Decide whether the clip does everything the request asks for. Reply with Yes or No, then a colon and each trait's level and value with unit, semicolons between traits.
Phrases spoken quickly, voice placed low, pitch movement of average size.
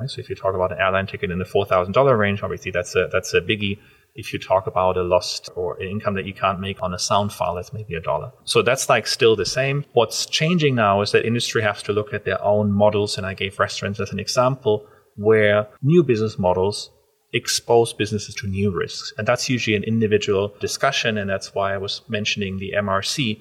Yes: fast, 225 wpm; low, 105 Hz; average, 3.2 semitones